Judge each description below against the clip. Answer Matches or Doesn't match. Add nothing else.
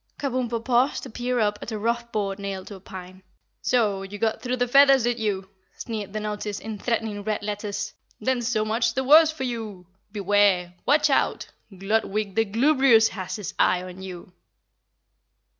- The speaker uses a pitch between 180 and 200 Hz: Doesn't match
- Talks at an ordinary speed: Matches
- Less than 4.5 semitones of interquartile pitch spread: Matches